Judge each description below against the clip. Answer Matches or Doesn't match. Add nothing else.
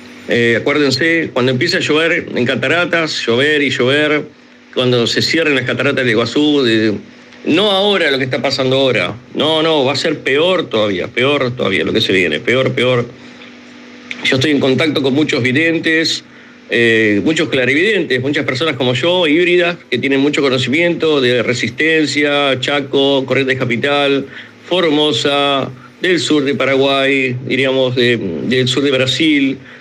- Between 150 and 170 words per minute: Matches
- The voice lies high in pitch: Doesn't match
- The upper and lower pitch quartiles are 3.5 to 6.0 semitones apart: Doesn't match